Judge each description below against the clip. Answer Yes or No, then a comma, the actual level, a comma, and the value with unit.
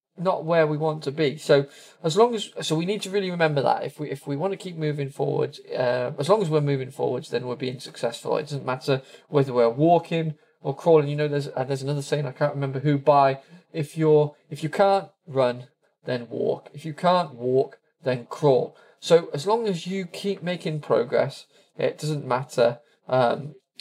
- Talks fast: Yes, fast, 210 wpm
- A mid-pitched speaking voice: Yes, medium, 150 Hz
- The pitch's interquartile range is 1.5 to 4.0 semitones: Yes, average, 3.7 semitones